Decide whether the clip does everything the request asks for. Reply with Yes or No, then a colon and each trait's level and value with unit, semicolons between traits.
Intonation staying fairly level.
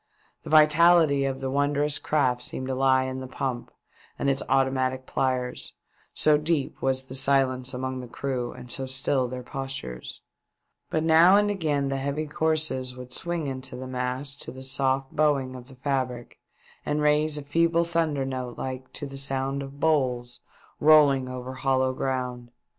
Yes: narrow, 2.3 semitones